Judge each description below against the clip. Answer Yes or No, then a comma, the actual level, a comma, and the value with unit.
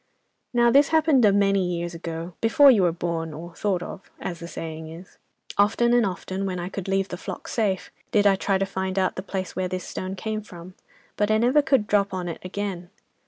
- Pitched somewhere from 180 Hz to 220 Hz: Yes, high, 190 Hz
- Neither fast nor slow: No, fast, 220 wpm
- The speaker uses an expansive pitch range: No, average, 2.9 semitones